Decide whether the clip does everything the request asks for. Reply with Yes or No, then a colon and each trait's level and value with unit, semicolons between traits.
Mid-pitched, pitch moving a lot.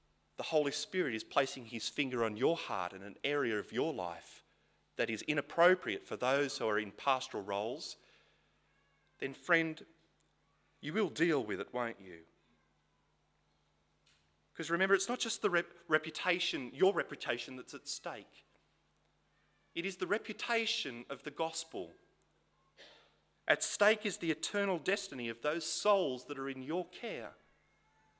Yes: medium, 155 Hz; wide, 6.5 semitones